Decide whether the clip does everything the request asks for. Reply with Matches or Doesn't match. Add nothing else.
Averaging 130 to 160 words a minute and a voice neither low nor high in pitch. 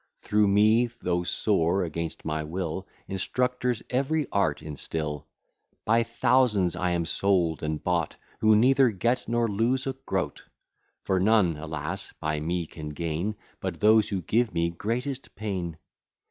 Doesn't match